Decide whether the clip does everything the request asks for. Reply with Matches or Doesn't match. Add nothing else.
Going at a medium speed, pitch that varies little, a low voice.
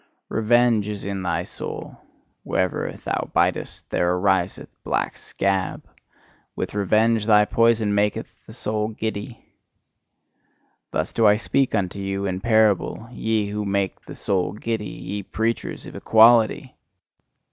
Doesn't match